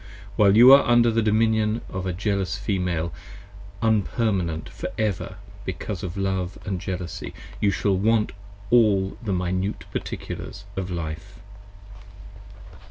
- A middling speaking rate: No, slow, 125 wpm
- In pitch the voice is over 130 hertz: No, low, 100 Hz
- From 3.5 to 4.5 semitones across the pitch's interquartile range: No, average, 3.1 semitones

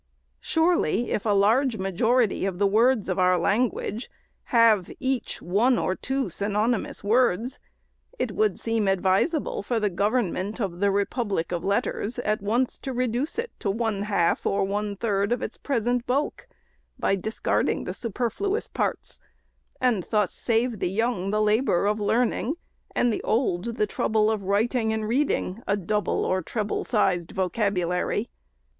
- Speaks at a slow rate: No, average, 155 wpm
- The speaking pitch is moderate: No, high, 215 Hz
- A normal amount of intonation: Yes, average, 3.6 semitones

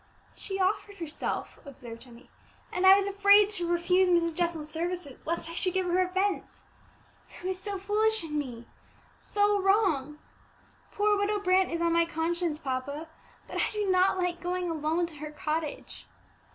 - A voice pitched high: Yes, very high, 350 Hz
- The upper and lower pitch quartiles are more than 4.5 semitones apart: No, average, 3.6 semitones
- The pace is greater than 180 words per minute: No, average, 165 wpm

